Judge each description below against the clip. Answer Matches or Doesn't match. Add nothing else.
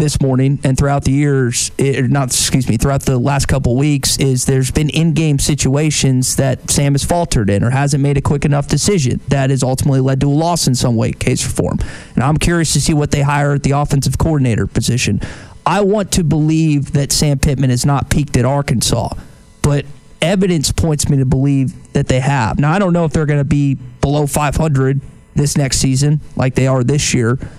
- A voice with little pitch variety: Matches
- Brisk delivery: Matches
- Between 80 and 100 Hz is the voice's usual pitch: Doesn't match